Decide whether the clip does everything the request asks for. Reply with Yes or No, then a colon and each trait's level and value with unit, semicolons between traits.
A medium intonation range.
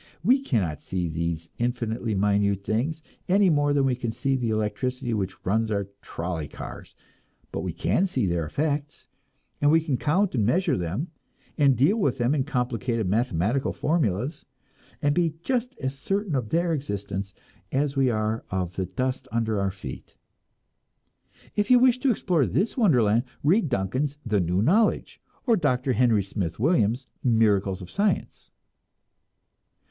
No: wide, 6.8 semitones